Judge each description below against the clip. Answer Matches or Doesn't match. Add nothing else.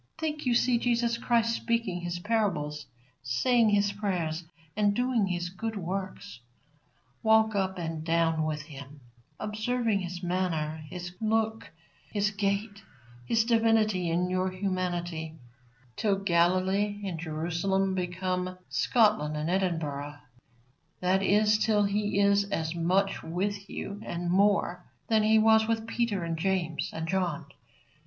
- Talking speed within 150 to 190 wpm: Doesn't match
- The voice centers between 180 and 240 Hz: Matches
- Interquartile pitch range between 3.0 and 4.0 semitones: Matches